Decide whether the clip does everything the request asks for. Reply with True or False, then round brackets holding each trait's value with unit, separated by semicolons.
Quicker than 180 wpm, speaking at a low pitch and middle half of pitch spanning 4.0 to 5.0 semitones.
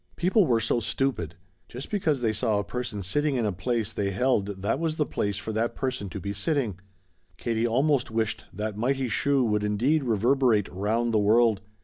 True (195 wpm; 115 Hz; 4.3 semitones)